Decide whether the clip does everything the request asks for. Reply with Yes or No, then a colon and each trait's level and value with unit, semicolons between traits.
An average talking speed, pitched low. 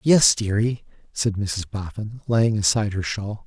Yes: average, 155 wpm; low, 105 Hz